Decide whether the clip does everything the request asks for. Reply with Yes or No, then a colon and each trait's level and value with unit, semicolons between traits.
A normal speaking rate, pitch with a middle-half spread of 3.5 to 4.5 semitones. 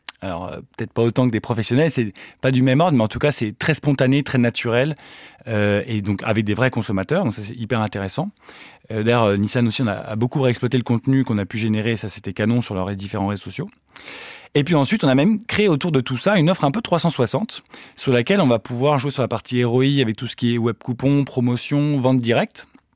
No: fast, 245 wpm; average, 3.9 semitones